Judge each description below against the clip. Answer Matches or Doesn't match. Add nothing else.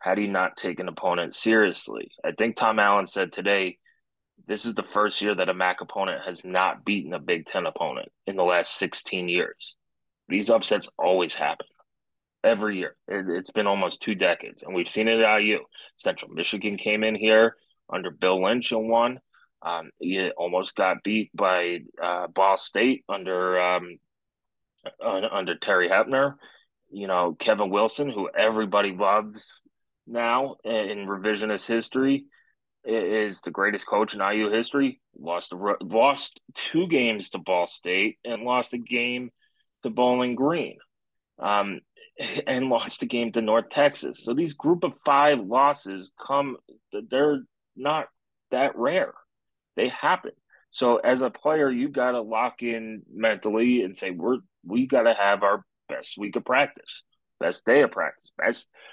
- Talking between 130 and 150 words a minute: Doesn't match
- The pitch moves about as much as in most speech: Matches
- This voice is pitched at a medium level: Doesn't match